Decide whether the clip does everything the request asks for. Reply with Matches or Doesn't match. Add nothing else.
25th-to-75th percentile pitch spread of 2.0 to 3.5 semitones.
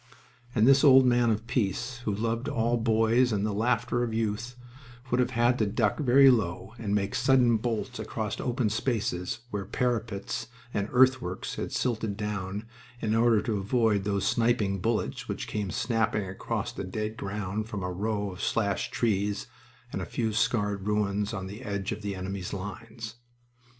Matches